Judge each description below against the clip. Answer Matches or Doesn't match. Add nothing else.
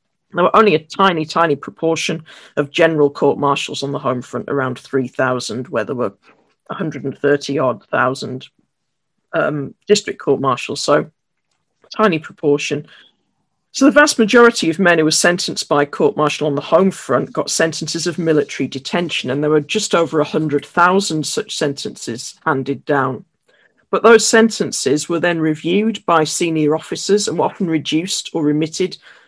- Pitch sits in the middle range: Matches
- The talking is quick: Doesn't match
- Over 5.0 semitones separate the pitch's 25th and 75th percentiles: Doesn't match